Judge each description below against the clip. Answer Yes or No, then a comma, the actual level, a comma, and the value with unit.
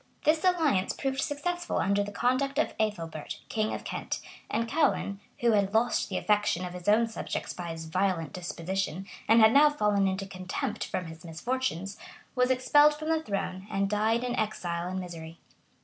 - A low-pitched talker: No, high, 210 Hz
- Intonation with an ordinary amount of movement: No, wide, 5.7 semitones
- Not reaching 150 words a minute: No, average, 170 wpm